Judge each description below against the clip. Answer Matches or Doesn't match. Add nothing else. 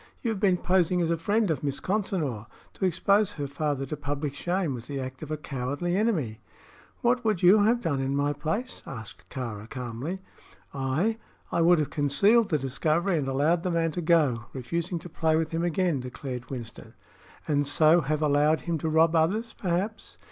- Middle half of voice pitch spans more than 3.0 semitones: Matches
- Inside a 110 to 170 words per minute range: Doesn't match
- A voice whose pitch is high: Doesn't match